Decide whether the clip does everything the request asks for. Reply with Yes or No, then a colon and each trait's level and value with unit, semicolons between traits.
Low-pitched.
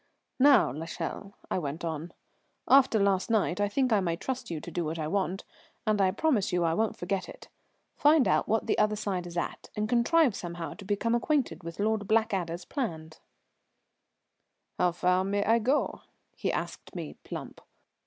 No: high, 200 Hz